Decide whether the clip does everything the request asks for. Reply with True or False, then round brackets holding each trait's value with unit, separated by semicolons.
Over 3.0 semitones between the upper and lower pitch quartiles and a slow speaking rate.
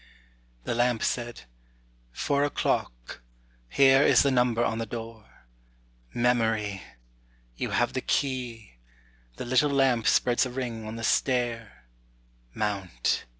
False (2.4 semitones; 125 wpm)